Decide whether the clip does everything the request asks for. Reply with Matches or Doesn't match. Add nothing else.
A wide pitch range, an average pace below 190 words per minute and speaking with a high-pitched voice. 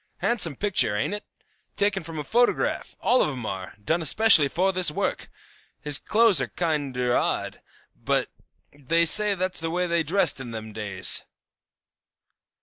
Doesn't match